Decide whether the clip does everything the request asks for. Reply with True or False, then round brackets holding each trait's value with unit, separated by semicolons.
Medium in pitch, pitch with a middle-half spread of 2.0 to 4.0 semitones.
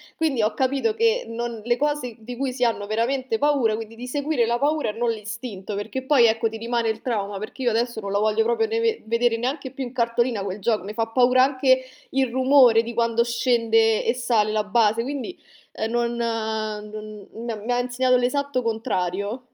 False (235 Hz; 2.8 semitones)